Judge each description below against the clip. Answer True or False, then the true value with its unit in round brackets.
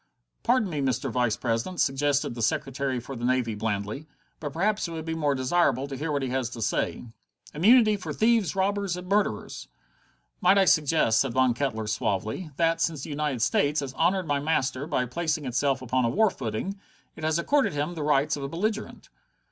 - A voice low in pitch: False (145 Hz)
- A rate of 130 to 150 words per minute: False (195 wpm)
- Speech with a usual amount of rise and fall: True (5.0 semitones)